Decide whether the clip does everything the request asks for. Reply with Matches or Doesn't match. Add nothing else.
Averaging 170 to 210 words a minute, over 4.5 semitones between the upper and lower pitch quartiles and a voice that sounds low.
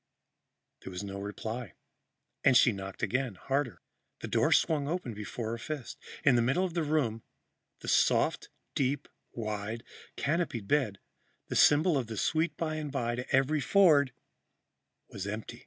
Doesn't match